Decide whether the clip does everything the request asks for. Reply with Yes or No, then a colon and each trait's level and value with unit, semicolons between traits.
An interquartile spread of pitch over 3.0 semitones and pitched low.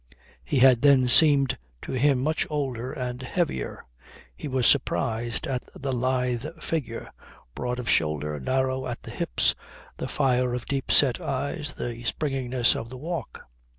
No: narrow, 2.5 semitones; low, 130 Hz